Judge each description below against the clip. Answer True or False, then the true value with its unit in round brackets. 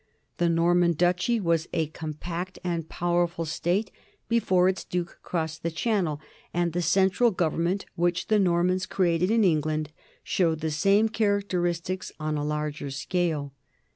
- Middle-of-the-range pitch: True (175 Hz)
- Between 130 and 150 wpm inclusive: True (140 wpm)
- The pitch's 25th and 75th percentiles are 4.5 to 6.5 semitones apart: False (2.6 semitones)